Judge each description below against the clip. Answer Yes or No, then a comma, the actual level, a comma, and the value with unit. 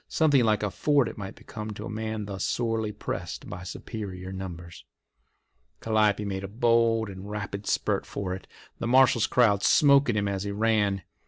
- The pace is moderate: Yes, average, 175 wpm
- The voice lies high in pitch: No, low, 105 Hz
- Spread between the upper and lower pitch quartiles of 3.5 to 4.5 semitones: No, narrow, 2.6 semitones